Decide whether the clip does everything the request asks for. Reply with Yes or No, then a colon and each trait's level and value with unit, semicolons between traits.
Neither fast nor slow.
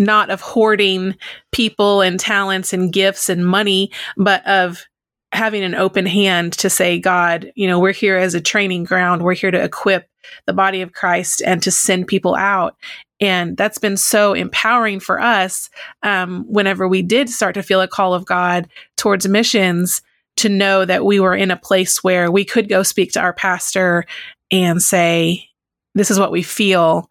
Yes: average, 185 wpm